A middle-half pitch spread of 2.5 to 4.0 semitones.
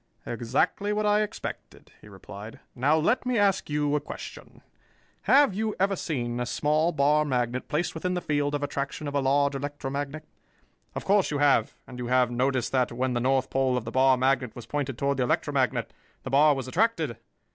Yes: average, 3.4 semitones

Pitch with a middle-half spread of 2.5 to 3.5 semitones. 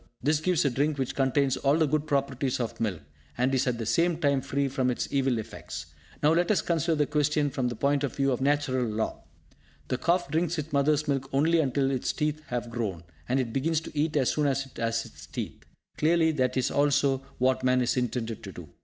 Yes: average, 3.0 semitones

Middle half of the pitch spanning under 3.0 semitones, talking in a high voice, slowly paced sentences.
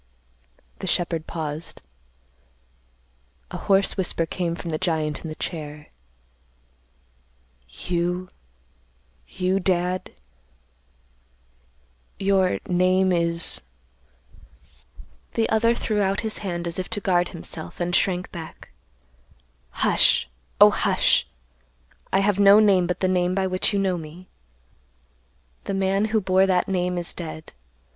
No: narrow, 2.4 semitones; medium, 180 Hz; slow, 115 wpm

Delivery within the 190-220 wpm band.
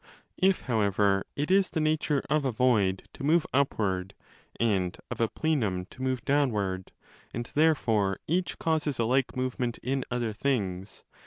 No: average, 155 wpm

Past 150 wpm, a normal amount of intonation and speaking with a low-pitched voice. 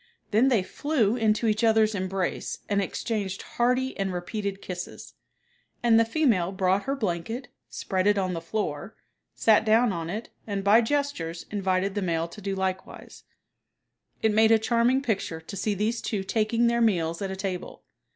No: average, 170 wpm; average, 3.4 semitones; high, 205 Hz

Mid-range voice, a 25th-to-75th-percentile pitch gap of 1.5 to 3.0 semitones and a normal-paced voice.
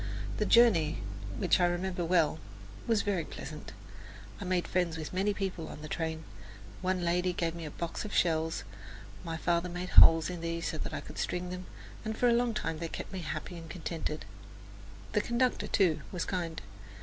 Yes: medium, 175 Hz; narrow, 2.4 semitones; average, 190 wpm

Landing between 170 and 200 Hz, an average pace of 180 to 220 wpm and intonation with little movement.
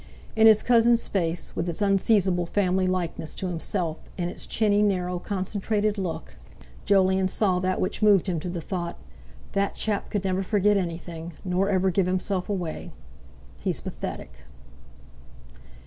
No: medium, 185 Hz; average, 145 wpm; narrow, 2.3 semitones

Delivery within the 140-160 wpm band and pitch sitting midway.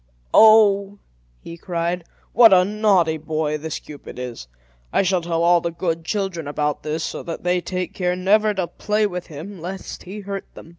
No: average, 185 wpm; medium, 180 Hz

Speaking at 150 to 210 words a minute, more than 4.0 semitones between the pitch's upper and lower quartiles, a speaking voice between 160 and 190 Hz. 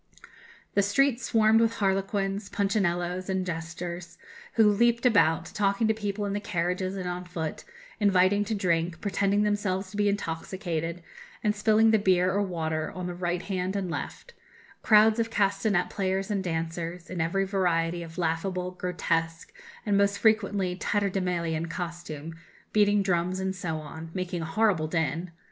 No: average, 155 wpm; average, 2.9 semitones; medium, 185 Hz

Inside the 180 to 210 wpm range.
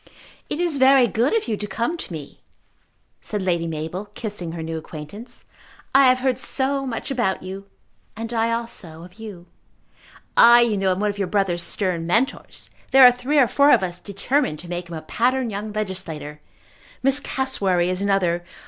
Yes: average, 185 wpm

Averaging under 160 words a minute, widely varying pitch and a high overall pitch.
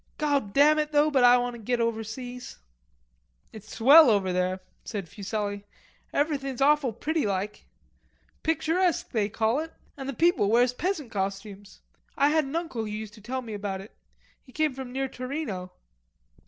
No: average, 165 wpm; wide, 5.9 semitones; high, 245 Hz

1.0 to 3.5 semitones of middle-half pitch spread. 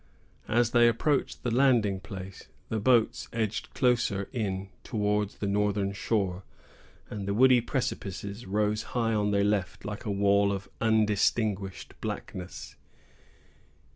Yes: narrow, 2.6 semitones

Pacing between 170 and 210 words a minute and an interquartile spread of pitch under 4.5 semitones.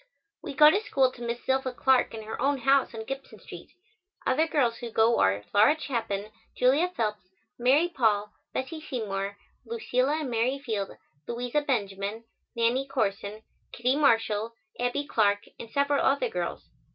No: average, 155 wpm; average, 4.1 semitones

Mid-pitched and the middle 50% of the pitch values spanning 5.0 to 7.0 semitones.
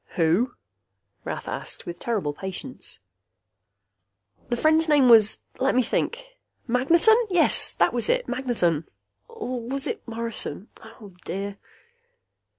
No: high, 240 Hz; wide, 5.4 semitones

